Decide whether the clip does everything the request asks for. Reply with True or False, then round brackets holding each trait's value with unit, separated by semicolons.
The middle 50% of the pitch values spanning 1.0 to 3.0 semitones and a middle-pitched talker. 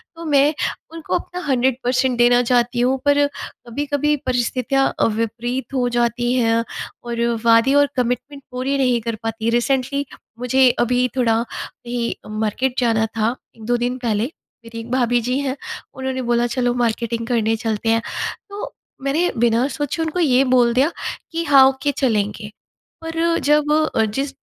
False (2.7 semitones; 245 Hz)